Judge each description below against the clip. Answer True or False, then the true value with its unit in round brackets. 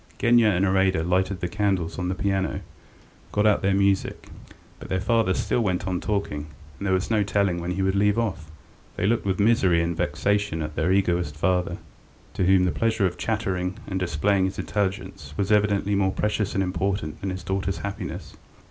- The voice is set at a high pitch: False (95 Hz)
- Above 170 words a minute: True (190 wpm)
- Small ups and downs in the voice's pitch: True (2.1 semitones)